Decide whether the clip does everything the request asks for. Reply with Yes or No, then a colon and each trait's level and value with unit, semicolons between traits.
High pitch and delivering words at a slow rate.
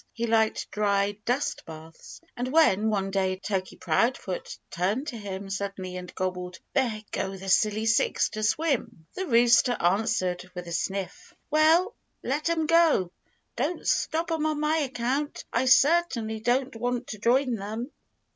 No: high, 225 Hz; average, 155 wpm